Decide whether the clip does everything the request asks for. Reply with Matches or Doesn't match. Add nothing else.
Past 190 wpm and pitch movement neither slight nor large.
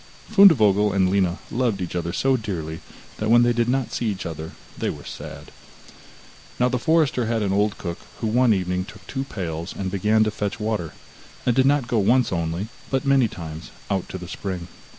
Matches